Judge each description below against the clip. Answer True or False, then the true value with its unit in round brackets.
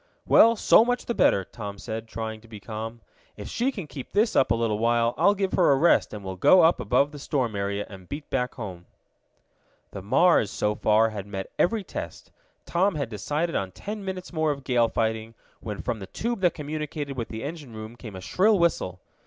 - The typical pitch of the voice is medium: False (120 Hz)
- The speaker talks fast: True (215 wpm)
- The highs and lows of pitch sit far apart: True (7.9 semitones)